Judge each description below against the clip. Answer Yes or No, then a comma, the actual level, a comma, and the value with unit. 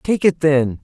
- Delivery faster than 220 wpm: No, fast, 215 wpm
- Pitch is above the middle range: No, medium, 150 Hz